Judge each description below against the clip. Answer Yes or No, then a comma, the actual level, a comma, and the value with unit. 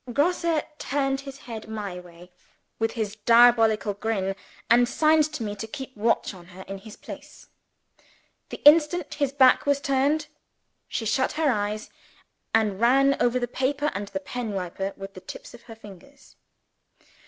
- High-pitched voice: Yes, high, 235 Hz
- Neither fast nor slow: Yes, average, 165 wpm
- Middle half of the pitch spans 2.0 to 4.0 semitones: No, average, 5.2 semitones